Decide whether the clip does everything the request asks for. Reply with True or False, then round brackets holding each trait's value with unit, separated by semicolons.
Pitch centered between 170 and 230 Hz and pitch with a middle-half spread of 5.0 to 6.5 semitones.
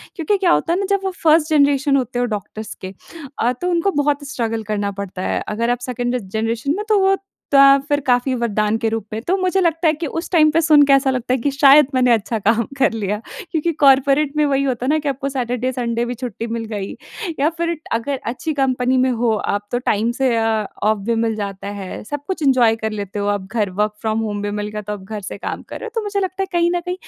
False (250 Hz; 5.3 semitones)